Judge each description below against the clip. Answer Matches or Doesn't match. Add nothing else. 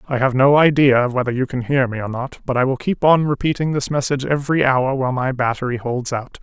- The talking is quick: Matches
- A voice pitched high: Doesn't match